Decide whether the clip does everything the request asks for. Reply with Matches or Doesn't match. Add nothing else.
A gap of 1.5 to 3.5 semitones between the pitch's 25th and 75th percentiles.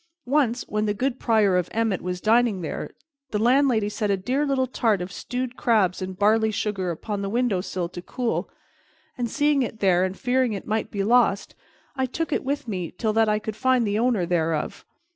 Doesn't match